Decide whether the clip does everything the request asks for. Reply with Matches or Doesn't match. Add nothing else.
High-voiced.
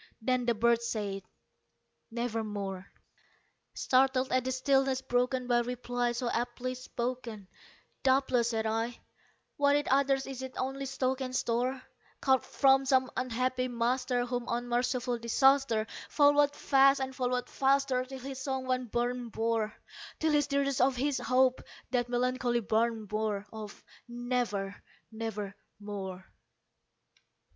Matches